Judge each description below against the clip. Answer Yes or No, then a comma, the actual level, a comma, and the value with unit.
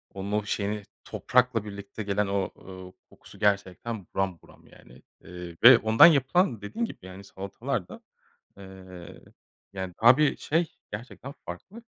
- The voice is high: No, low, 100 Hz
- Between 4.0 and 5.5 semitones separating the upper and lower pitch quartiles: Yes, average, 4.4 semitones